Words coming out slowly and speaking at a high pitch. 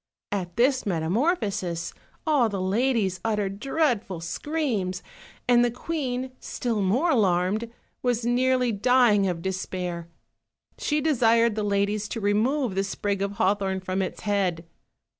Yes: slow, 130 wpm; high, 210 Hz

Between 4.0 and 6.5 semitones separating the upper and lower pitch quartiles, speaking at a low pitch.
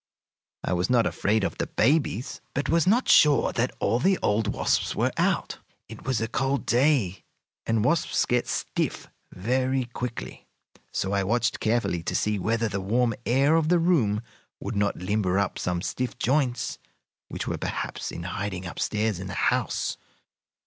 Yes: average, 4.6 semitones; low, 115 Hz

